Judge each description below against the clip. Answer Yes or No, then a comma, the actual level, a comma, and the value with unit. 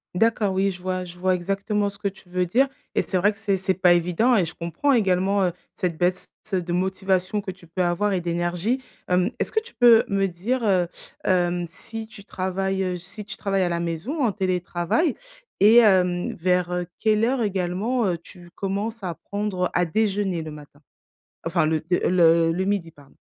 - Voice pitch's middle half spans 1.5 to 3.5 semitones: Yes, average, 2.8 semitones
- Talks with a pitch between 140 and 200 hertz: Yes, medium, 185 Hz